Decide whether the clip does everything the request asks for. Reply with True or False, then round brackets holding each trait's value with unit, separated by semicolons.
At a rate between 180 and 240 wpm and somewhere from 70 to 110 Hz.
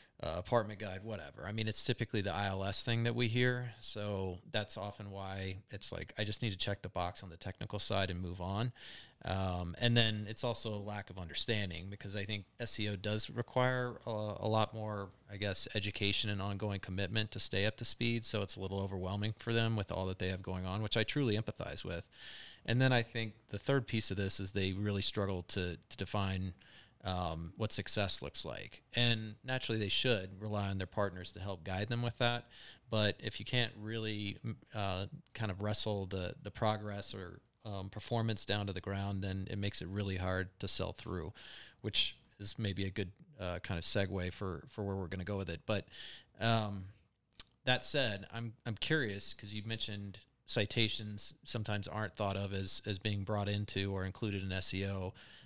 True (205 wpm; 105 Hz)